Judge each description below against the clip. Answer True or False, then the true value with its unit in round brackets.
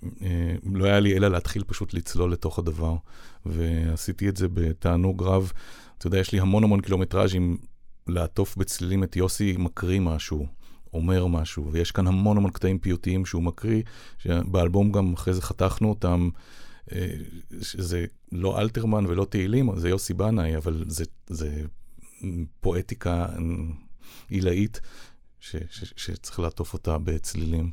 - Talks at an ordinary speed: True (130 wpm)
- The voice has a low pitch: True (90 Hz)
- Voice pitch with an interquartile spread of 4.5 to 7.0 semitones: False (2.5 semitones)